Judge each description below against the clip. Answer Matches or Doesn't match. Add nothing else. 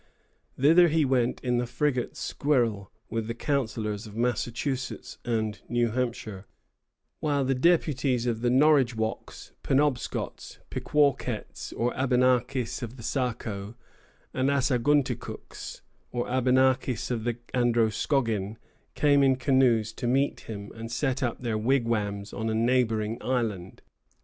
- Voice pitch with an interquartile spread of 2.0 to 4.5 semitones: Matches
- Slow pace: Matches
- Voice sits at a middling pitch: Doesn't match